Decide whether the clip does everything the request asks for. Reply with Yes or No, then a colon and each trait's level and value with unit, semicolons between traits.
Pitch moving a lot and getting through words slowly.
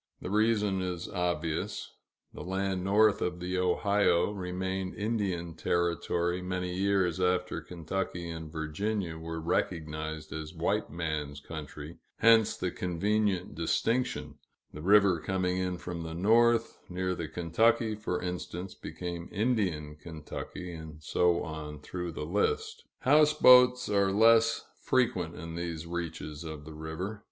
No: average, 3.4 semitones; slow, 130 wpm